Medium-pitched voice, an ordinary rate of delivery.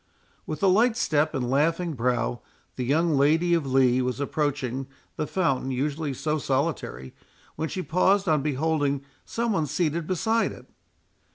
Yes: medium, 150 Hz; average, 155 wpm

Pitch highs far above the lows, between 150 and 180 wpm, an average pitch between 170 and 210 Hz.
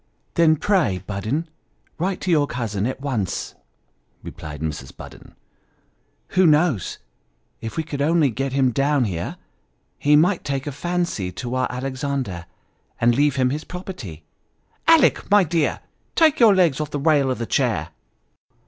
No: wide, 5.7 semitones; average, 160 wpm; medium, 140 Hz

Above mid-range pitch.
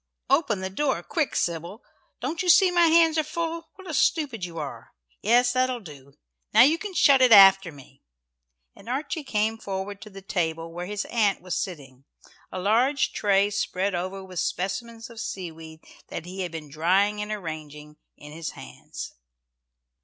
Yes: high, 200 Hz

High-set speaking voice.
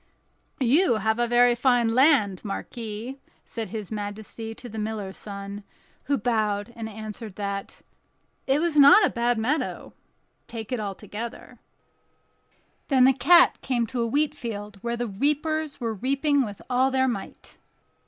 Yes: high, 235 Hz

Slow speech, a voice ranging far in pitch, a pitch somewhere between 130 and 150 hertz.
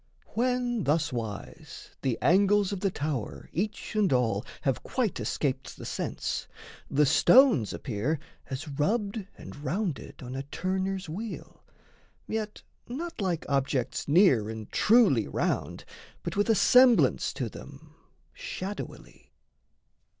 No: slow, 120 wpm; wide, 7.8 semitones; medium, 180 Hz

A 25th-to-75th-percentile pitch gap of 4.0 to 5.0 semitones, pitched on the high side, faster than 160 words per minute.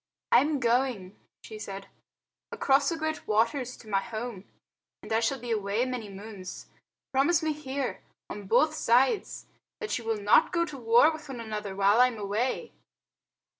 Yes: average, 4.6 semitones; high, 235 Hz; average, 170 wpm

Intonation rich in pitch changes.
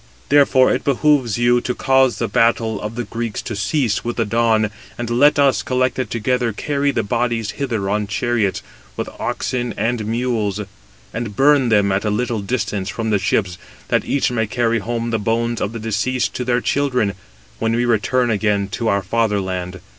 No: average, 2.8 semitones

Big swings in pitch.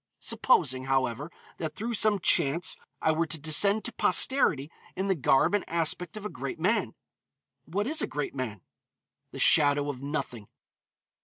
Yes: wide, 6.4 semitones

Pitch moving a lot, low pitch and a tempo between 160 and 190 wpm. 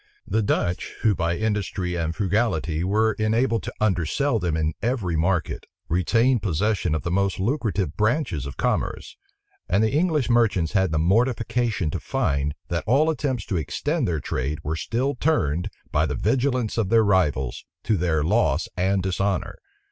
Yes: wide, 5.7 semitones; low, 100 Hz; average, 165 wpm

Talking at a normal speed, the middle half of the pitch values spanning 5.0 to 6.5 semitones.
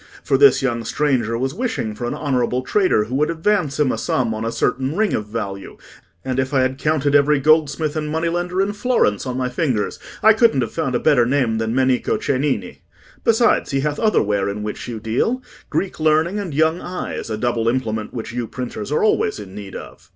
No: fast, 210 wpm; wide, 5.4 semitones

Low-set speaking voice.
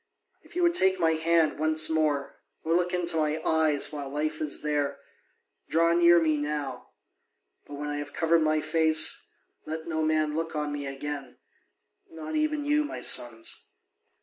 No: medium, 155 Hz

